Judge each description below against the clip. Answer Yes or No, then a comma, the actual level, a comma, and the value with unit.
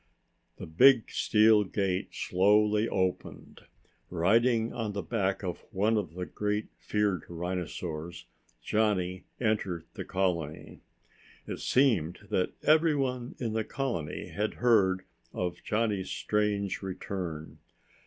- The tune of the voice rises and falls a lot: No, average, 3.5 semitones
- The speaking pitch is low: Yes, low, 100 Hz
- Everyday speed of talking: No, slow, 115 wpm